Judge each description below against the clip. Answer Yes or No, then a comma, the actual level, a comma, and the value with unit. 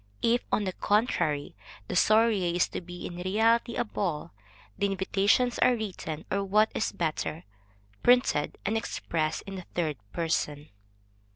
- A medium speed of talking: Yes, average, 150 wpm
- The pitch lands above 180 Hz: Yes, high, 190 Hz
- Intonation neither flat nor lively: Yes, average, 4.6 semitones